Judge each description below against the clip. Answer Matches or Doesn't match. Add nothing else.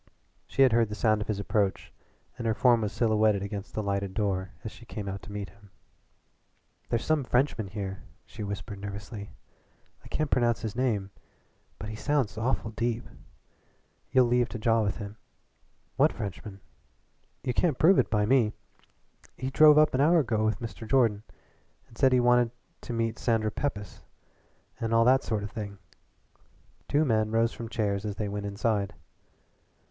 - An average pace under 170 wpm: Doesn't match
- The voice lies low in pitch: Matches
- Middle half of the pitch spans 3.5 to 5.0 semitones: Doesn't match